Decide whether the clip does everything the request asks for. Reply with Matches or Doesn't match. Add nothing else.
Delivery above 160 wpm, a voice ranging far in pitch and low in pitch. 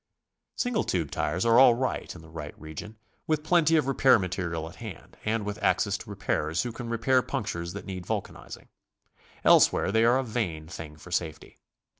Matches